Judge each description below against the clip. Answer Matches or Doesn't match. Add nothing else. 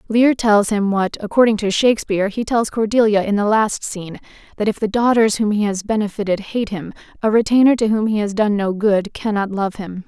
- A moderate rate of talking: Doesn't match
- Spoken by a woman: Matches